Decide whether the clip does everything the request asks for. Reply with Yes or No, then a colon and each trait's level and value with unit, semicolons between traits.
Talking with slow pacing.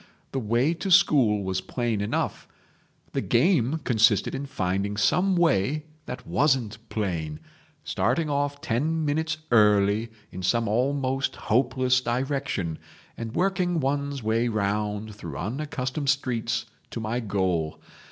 Yes: slow, 125 wpm